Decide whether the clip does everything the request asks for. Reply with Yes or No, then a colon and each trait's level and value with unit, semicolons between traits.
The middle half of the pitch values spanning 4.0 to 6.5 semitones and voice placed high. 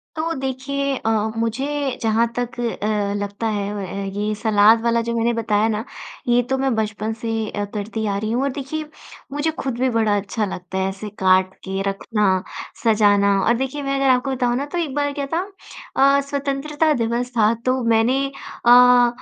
Yes: average, 4.3 semitones; high, 230 Hz